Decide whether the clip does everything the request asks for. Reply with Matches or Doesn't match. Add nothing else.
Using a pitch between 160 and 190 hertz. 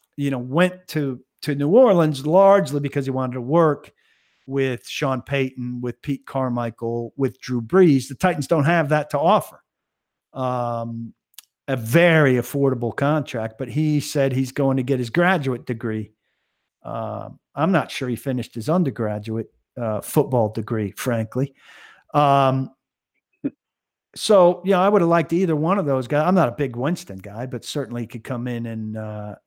Doesn't match